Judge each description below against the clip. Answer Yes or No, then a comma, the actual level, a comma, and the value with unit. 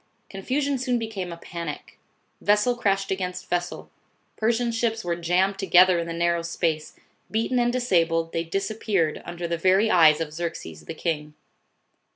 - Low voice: No, medium, 180 Hz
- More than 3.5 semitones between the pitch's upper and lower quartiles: Yes, average, 4.5 semitones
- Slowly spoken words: No, average, 155 wpm